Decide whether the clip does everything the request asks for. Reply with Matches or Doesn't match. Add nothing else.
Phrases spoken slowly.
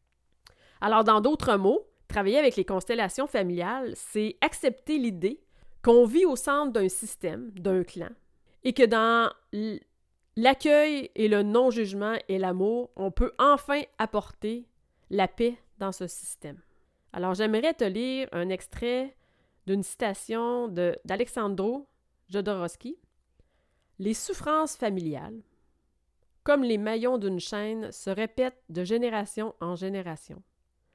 Matches